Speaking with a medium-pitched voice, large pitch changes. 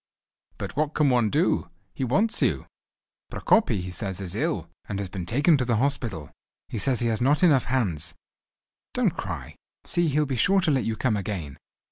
No: low, 120 Hz; wide, 6.3 semitones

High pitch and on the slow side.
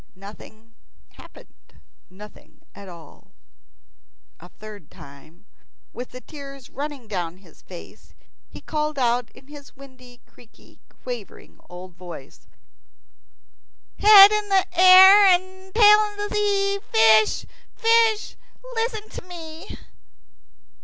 Yes: very high, 270 Hz; slow, 105 wpm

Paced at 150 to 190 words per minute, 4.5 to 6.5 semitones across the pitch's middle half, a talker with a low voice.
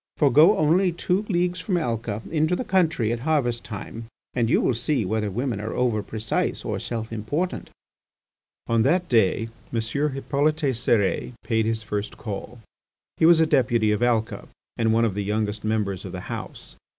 Yes: average, 175 wpm; wide, 5.6 semitones; low, 120 Hz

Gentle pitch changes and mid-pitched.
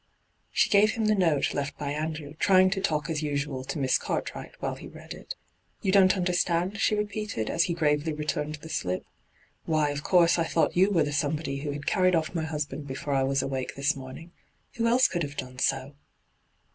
No: average, 4.3 semitones; medium, 155 Hz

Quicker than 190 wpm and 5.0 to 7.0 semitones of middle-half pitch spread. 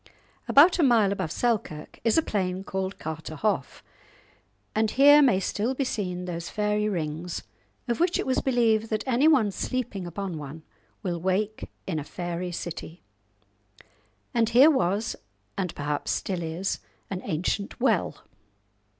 No: average, 140 wpm; average, 5.3 semitones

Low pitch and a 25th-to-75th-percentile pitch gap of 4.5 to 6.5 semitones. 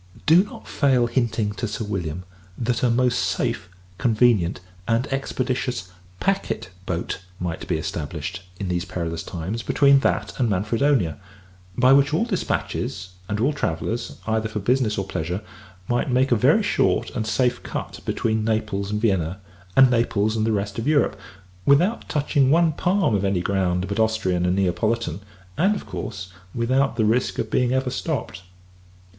Yes: low, 110 Hz; average, 5.1 semitones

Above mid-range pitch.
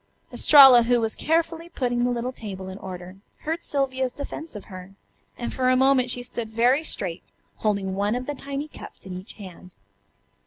Yes: high, 245 Hz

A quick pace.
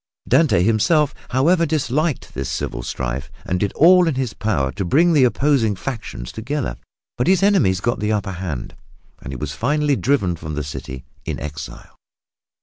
No: average, 170 wpm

